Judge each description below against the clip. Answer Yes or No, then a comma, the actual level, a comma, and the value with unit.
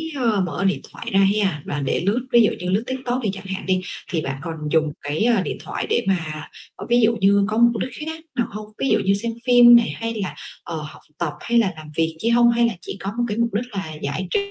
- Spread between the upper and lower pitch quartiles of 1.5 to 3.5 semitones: No, average, 5.2 semitones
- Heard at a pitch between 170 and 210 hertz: Yes, high, 200 Hz